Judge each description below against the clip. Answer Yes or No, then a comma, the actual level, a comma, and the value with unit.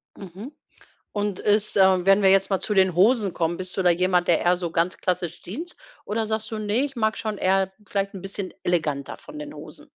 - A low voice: No, high, 195 Hz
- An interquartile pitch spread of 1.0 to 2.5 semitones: No, average, 2.9 semitones